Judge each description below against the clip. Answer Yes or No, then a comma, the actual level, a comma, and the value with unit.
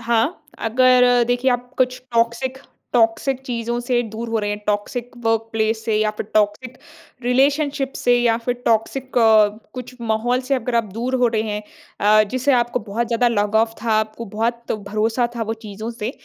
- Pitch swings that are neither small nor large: No, narrow, 2.1 semitones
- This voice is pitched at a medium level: No, high, 235 Hz